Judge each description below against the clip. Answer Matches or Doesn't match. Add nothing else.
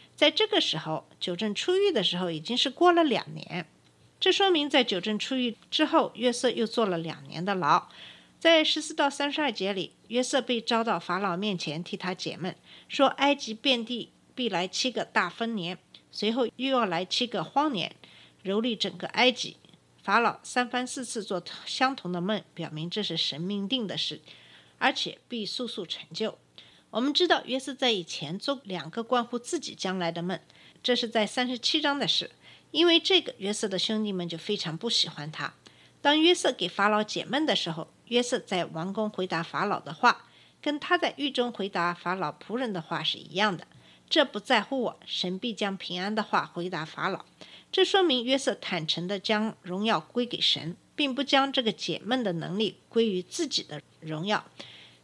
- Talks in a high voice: Matches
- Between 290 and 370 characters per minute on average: Doesn't match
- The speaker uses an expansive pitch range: Matches